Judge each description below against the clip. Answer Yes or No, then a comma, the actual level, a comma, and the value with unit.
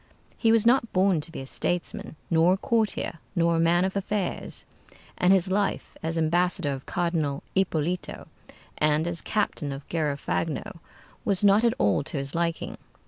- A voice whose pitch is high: No, medium, 170 Hz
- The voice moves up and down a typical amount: Yes, average, 3.6 semitones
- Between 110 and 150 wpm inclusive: No, average, 165 wpm